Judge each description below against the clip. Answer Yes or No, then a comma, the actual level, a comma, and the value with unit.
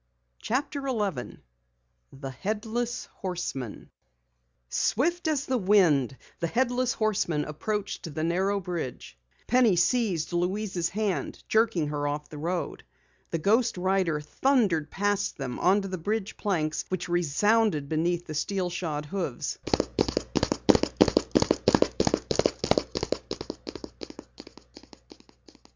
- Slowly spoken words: Yes, slow, 100 wpm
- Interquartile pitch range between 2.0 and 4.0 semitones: No, wide, 5.6 semitones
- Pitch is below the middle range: No, medium, 185 Hz